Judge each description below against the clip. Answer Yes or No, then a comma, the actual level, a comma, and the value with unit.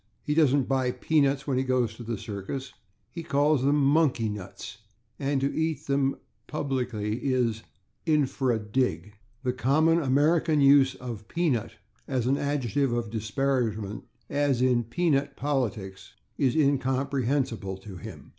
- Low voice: Yes, low, 130 Hz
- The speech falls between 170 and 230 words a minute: No, slow, 135 wpm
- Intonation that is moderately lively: Yes, average, 3.5 semitones